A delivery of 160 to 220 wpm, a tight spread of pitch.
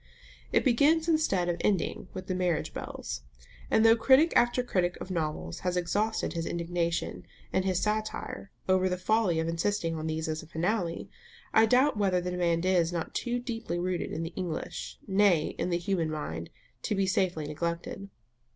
No: average, 180 wpm; average, 4.0 semitones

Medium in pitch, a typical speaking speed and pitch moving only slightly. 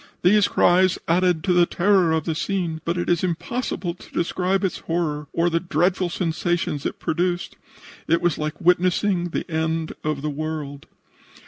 Yes: medium, 175 Hz; average, 165 wpm; narrow, 2.2 semitones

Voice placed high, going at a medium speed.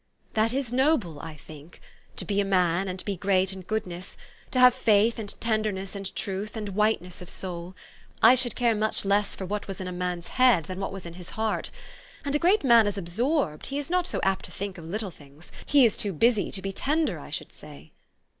No: high, 200 Hz; fast, 225 wpm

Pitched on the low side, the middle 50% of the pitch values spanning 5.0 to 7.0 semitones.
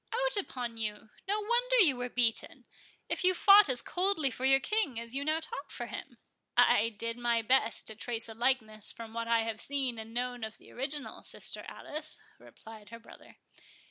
No: high, 245 Hz; average, 5.3 semitones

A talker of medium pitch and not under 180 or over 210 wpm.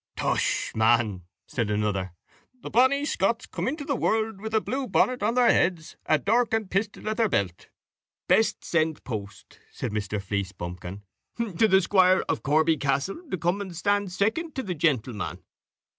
No: medium, 180 Hz; average, 170 wpm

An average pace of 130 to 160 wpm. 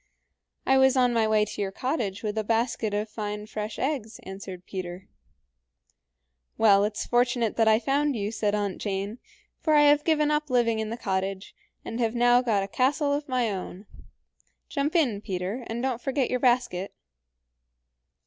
No: average, 170 wpm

